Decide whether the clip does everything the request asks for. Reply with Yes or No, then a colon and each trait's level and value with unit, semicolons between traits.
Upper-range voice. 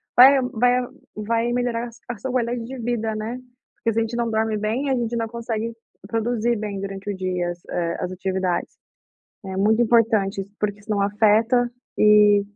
Yes: high, 225 Hz